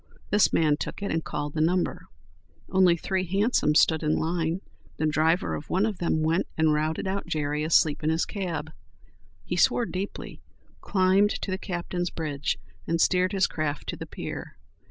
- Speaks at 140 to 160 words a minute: No, average, 175 wpm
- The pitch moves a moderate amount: Yes, average, 3.2 semitones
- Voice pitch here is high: No, medium, 165 Hz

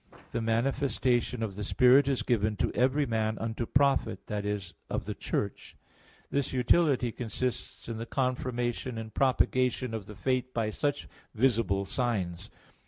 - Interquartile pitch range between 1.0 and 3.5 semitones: Yes, average, 2.9 semitones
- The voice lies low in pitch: Yes, low, 120 Hz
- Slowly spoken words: No, average, 155 wpm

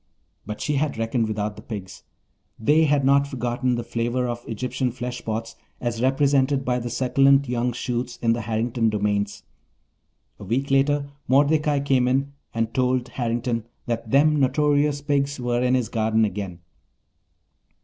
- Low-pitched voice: Yes, low, 125 Hz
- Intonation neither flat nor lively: Yes, average, 3.3 semitones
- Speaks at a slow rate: No, average, 150 wpm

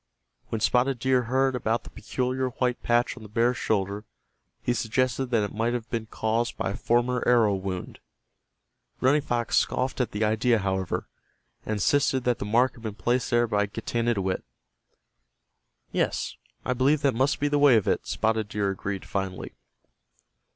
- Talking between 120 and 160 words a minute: No, average, 170 wpm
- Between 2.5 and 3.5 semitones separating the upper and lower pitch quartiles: Yes, average, 3.1 semitones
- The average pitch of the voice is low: Yes, low, 120 Hz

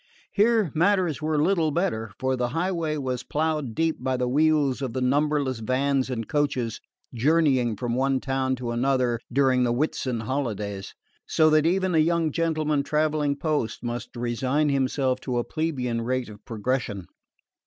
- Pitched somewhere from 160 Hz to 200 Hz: No, low, 135 Hz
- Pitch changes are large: No, average, 4.0 semitones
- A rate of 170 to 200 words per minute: No, average, 160 wpm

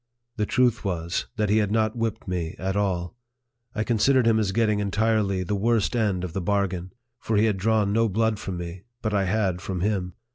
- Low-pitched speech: Yes, low, 105 Hz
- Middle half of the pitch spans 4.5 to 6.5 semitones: No, average, 3.0 semitones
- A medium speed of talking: No, fast, 215 wpm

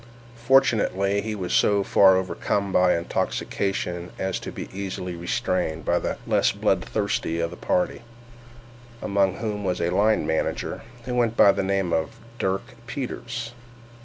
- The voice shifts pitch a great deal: No, average, 3.2 semitones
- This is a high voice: No, very low, 95 Hz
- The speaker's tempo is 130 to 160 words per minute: Yes, average, 145 wpm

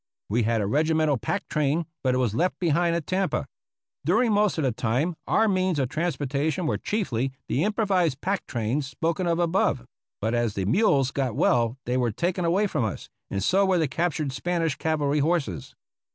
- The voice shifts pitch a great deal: Yes, wide, 5.7 semitones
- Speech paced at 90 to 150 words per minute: No, average, 190 wpm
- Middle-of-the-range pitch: Yes, medium, 155 Hz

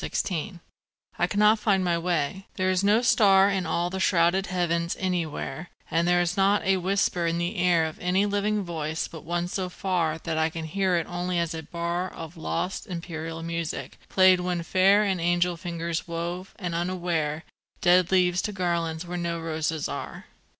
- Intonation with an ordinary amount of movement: No, narrow, 2.0 semitones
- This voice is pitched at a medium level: Yes, medium, 175 Hz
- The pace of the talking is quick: No, average, 185 wpm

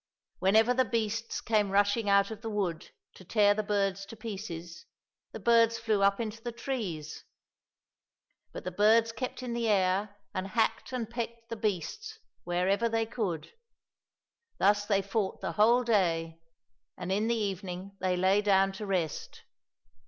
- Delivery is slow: No, average, 160 wpm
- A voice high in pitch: Yes, high, 205 Hz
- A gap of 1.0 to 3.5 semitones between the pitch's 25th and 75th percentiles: Yes, average, 3.0 semitones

